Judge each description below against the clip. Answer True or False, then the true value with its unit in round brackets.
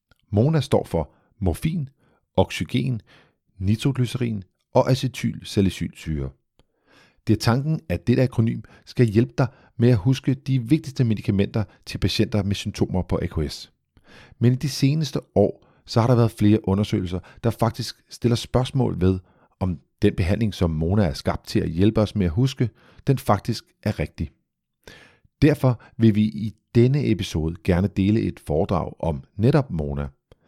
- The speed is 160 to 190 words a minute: False (150 wpm)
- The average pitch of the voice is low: True (110 Hz)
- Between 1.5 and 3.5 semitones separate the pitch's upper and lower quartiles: False (4.9 semitones)